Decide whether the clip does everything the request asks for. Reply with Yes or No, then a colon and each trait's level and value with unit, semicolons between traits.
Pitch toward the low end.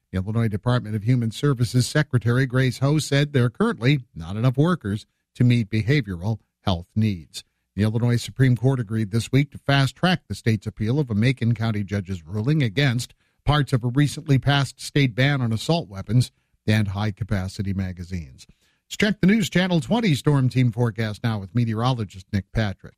Yes: low, 120 Hz